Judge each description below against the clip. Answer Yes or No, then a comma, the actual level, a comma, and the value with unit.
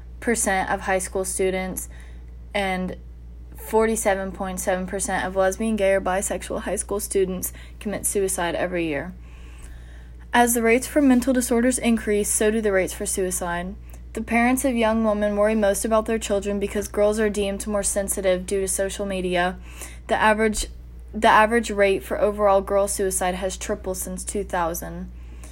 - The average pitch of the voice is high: Yes, high, 195 Hz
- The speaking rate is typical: Yes, average, 155 wpm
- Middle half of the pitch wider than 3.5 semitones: No, average, 2.7 semitones